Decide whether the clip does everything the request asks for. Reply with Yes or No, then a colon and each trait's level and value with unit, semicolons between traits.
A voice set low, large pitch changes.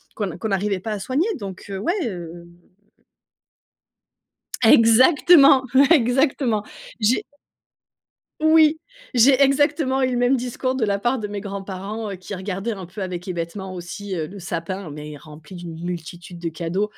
No: high, 200 Hz; wide, 5.9 semitones